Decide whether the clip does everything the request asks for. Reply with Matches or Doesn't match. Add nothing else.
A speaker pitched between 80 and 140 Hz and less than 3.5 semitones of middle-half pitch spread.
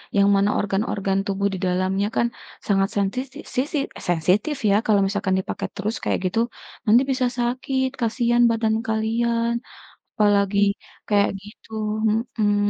Doesn't match